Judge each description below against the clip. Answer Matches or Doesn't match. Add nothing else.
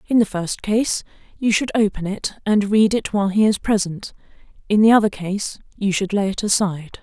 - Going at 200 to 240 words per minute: Matches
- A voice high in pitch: Matches